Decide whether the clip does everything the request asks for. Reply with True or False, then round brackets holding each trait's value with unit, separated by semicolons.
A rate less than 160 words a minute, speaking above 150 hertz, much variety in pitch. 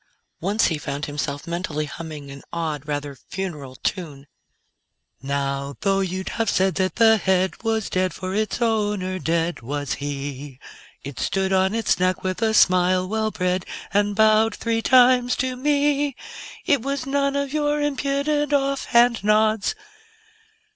True (150 wpm; 190 Hz; 6.7 semitones)